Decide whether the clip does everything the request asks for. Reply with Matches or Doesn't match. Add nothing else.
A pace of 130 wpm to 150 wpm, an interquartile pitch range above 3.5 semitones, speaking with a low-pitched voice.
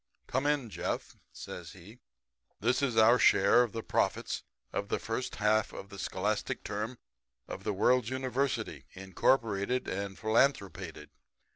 Matches